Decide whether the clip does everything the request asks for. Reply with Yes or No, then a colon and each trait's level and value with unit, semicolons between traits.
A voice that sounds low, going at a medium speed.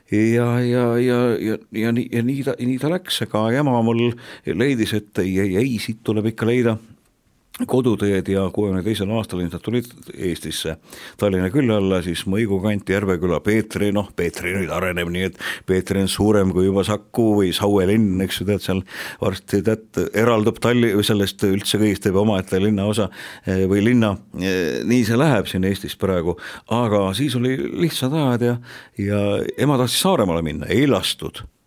Yes: low, 105 Hz; average, 175 wpm